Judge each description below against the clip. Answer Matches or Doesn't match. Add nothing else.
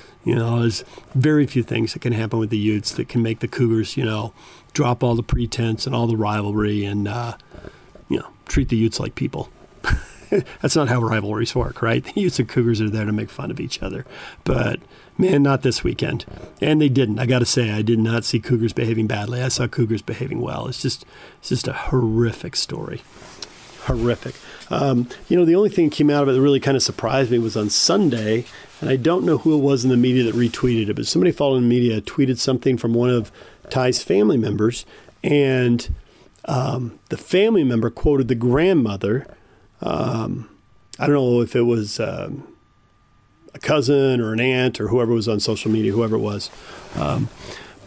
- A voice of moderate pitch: Doesn't match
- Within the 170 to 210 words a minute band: Matches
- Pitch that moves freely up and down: Doesn't match